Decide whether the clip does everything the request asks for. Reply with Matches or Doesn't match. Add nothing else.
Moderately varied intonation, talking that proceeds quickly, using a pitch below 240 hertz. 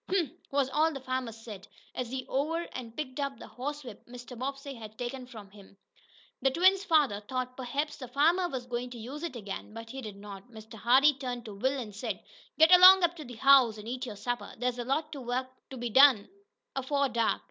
Doesn't match